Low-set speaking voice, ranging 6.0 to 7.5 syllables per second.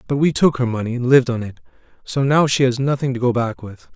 Yes: low, 125 Hz; 6.3 syllables/s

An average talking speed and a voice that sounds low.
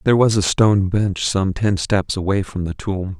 No: fast, 225 wpm; low, 100 Hz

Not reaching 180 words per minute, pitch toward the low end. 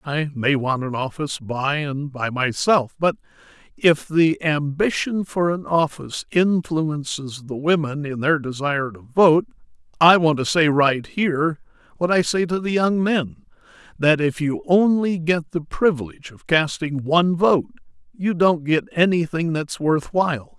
No: average, 165 wpm; medium, 155 Hz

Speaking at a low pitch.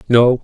Yes: low, 120 Hz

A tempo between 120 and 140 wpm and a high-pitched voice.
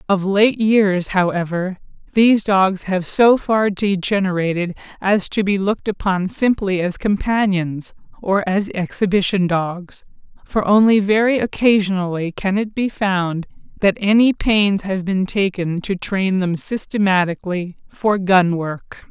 Yes: slow, 135 wpm; high, 195 Hz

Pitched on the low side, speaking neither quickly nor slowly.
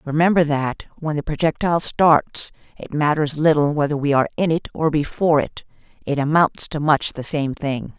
No: medium, 150 Hz; average, 180 wpm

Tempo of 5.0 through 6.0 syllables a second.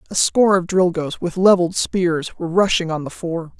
Yes: 5.4 syllables/s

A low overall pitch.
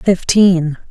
No: medium, 180 Hz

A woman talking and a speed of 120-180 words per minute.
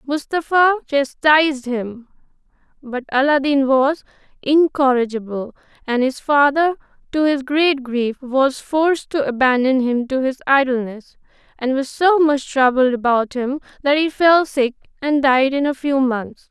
Yes: female; average, 140 wpm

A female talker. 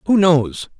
Yes: female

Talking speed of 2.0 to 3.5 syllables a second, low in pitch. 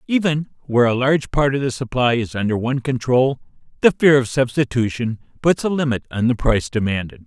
No: 5.9 syllables/s; low, 125 Hz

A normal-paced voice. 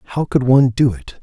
No: fast, 245 wpm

